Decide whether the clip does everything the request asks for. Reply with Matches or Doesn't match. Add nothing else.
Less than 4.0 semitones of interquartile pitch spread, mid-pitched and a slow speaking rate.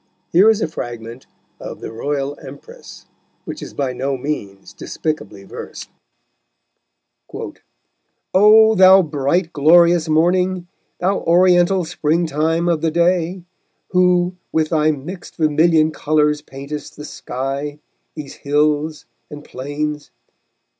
Matches